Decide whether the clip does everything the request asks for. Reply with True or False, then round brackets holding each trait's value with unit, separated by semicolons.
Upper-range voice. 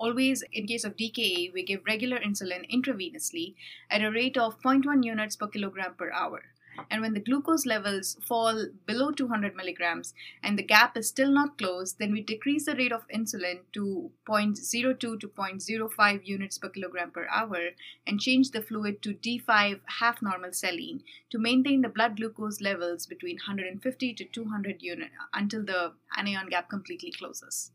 True (215 Hz)